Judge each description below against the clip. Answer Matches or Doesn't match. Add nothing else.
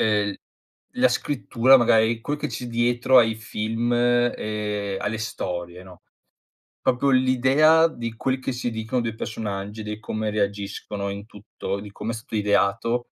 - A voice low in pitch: Matches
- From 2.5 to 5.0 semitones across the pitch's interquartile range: Matches